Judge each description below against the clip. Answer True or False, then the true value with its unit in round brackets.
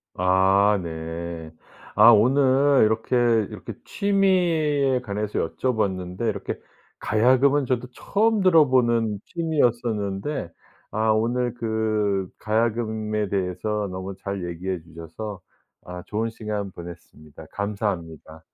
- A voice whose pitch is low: True (110 Hz)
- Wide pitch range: False (4.8 semitones)